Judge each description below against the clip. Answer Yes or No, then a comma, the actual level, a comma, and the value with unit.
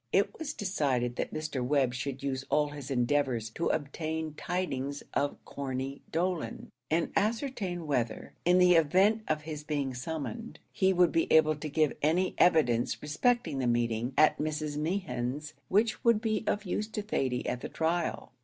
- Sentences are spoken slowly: No, average, 165 wpm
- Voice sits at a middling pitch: Yes, medium, 155 Hz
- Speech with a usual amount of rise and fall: Yes, average, 5.0 semitones